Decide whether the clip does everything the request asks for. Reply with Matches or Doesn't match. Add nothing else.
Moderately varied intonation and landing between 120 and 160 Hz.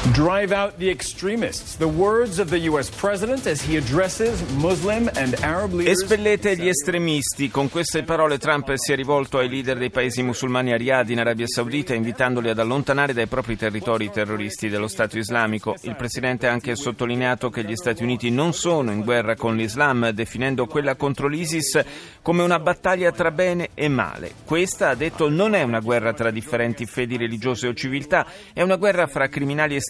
Doesn't match